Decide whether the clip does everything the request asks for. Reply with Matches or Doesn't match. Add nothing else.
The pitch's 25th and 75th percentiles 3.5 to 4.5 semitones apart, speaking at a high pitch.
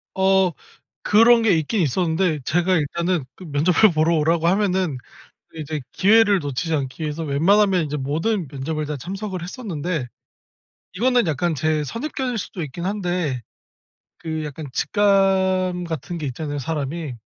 Doesn't match